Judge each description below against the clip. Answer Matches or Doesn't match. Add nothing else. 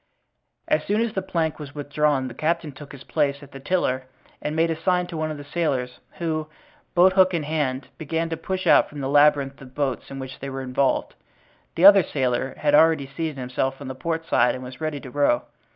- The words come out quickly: Matches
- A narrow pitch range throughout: Doesn't match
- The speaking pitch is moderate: Matches